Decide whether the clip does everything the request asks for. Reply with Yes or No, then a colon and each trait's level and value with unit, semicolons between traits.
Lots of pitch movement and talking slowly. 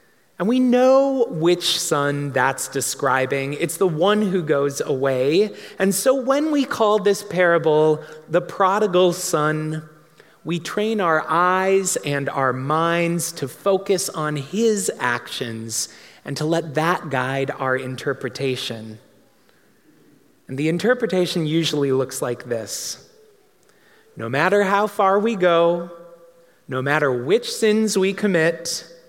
Yes: wide, 5.7 semitones; slow, 125 wpm